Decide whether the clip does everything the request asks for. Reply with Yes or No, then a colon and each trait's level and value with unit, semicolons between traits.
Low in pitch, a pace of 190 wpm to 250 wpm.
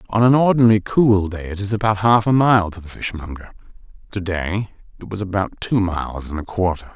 Yes: low, 100 Hz; fast, 205 wpm